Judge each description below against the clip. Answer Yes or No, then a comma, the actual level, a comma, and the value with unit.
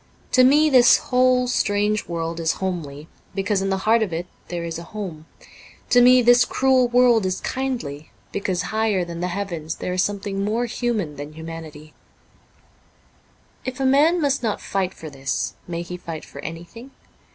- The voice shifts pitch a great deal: Yes, wide, 6.5 semitones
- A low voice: No, high, 195 Hz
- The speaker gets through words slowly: No, average, 175 wpm